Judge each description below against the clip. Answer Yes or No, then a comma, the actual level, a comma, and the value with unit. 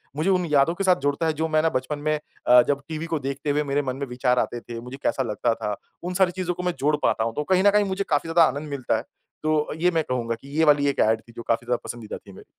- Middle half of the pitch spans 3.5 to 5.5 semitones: Yes, average, 4.6 semitones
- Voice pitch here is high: No, medium, 145 Hz